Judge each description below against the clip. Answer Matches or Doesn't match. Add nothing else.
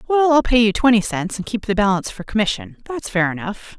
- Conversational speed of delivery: Doesn't match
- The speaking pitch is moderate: Doesn't match